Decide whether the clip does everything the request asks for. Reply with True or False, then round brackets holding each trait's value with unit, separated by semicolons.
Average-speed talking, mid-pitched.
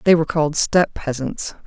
True (180 wpm; 160 Hz)